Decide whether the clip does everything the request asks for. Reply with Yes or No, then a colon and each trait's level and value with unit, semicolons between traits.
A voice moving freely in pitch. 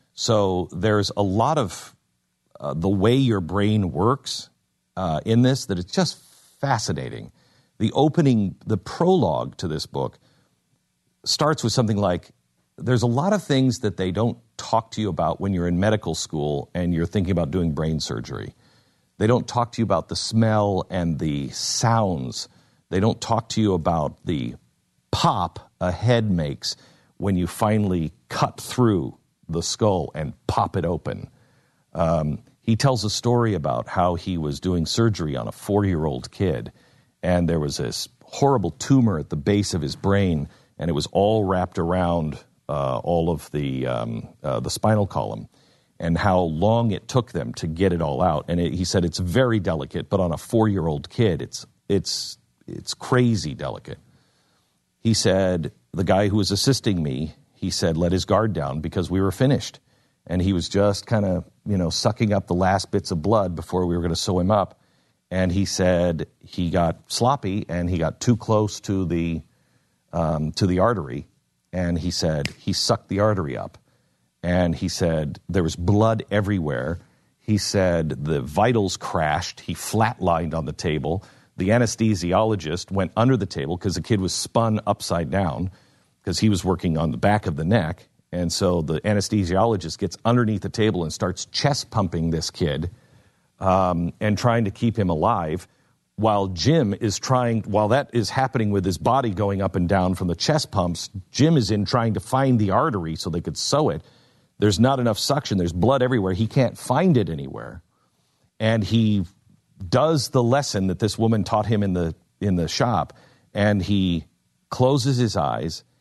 No: average, 4.7 semitones